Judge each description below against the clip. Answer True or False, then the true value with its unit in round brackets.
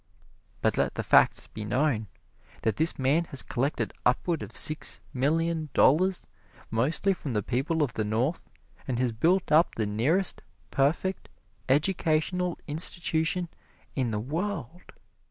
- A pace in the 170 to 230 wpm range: False (135 wpm)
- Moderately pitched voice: True (150 Hz)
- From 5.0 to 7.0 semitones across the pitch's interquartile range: True (5.4 semitones)